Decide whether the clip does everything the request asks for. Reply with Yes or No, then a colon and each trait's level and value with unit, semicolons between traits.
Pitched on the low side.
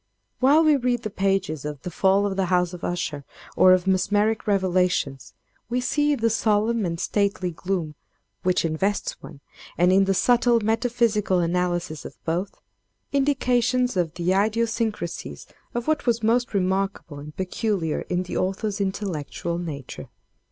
No: high, 195 Hz